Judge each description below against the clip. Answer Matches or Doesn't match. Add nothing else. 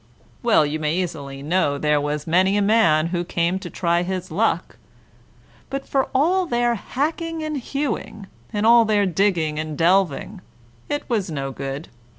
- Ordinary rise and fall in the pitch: Doesn't match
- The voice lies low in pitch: Doesn't match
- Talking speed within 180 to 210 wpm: Doesn't match